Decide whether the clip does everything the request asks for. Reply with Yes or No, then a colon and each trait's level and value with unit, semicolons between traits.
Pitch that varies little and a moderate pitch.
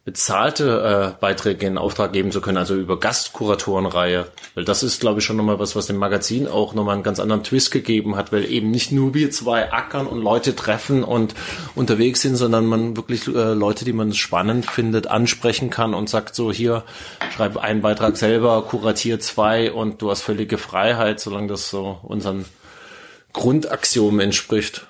No: narrow, 2.3 semitones; low, 110 Hz